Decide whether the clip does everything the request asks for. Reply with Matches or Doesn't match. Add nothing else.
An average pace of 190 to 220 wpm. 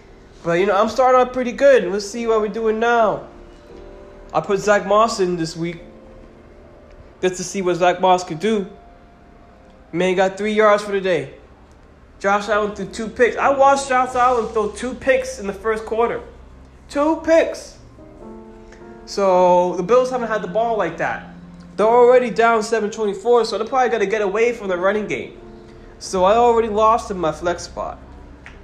Doesn't match